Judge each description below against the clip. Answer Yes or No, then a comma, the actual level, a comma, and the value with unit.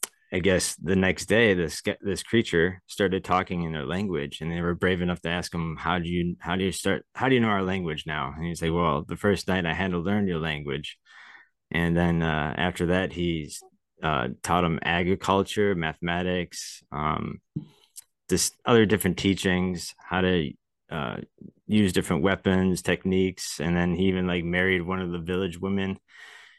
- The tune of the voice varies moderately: No, narrow, 2.0 semitones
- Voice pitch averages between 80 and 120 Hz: Yes, very low, 90 Hz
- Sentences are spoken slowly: No, average, 185 wpm